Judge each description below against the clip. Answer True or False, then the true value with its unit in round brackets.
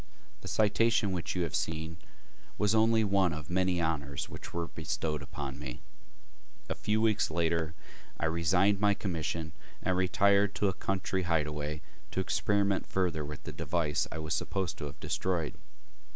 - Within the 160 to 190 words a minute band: True (165 wpm)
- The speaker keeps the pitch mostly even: False (4.0 semitones)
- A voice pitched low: True (85 Hz)